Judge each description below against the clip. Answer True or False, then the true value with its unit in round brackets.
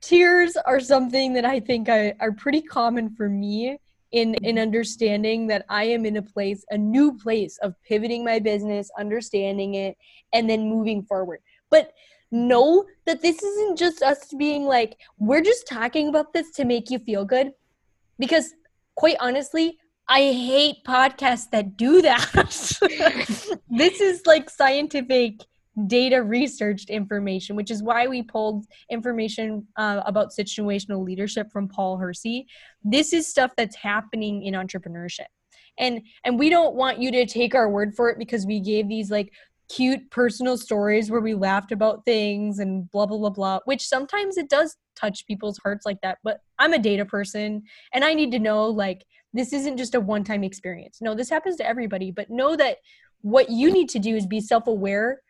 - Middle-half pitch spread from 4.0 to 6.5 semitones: True (4.7 semitones)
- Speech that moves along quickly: False (175 wpm)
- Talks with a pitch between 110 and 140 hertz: False (230 Hz)